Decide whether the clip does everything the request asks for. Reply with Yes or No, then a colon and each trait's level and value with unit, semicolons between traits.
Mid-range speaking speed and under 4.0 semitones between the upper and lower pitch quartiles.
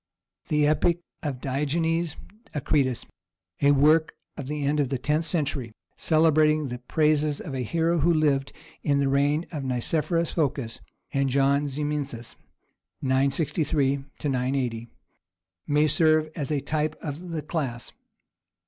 No: slow, 130 wpm; narrow, 2.4 semitones